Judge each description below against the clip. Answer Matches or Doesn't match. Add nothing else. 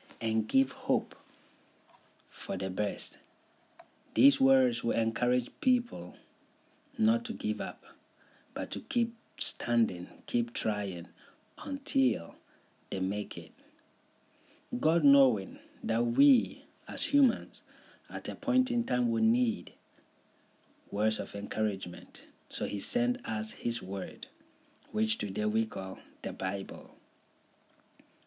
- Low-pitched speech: Doesn't match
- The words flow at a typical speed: Doesn't match